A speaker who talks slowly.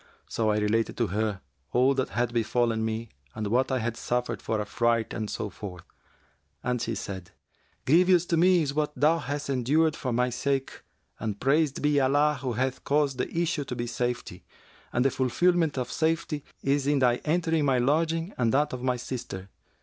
No: average, 190 wpm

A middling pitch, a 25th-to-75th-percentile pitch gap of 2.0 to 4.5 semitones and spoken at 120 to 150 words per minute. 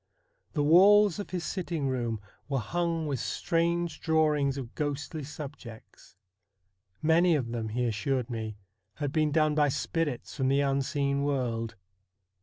Yes: medium, 145 Hz; average, 3.9 semitones; average, 140 wpm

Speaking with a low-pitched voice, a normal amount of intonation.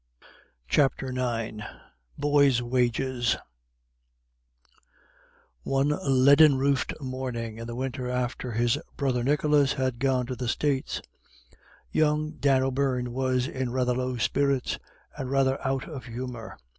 No: low, 130 Hz; narrow, 1.8 semitones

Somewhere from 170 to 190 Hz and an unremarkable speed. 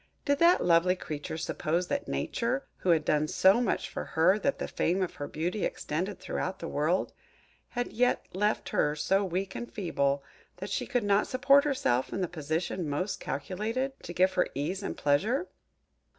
Yes: medium, 185 Hz; average, 180 wpm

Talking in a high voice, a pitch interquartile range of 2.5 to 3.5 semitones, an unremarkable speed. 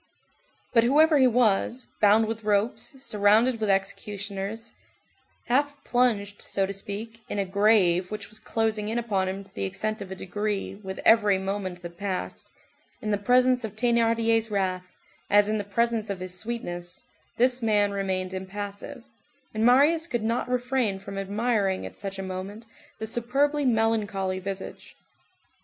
Yes: high, 210 Hz; average, 3.1 semitones; average, 155 wpm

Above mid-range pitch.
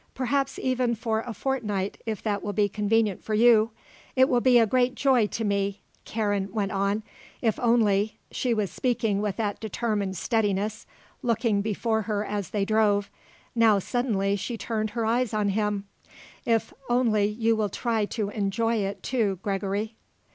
Yes: high, 215 Hz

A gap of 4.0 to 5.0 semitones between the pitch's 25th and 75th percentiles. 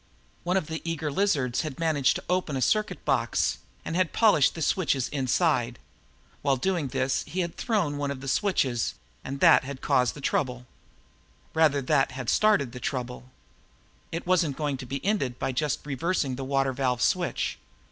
Yes: average, 4.4 semitones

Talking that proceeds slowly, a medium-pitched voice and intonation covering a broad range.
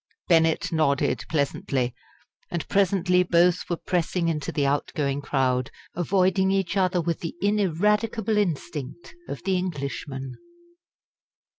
No: slow, 120 wpm; medium, 170 Hz; average, 4.7 semitones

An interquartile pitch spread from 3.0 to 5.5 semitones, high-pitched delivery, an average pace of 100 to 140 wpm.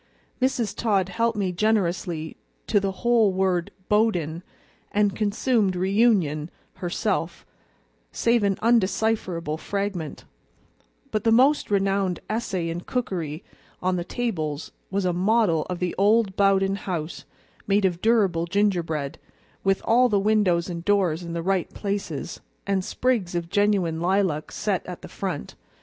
Yes: average, 3.5 semitones; high, 195 Hz; slow, 135 wpm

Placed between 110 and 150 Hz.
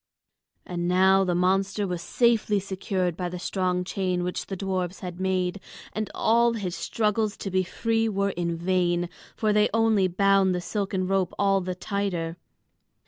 No: high, 190 Hz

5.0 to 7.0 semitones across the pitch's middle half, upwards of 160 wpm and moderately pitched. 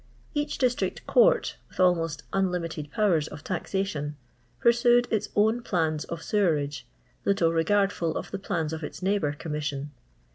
No: average, 5.3 semitones; average, 155 wpm; medium, 170 Hz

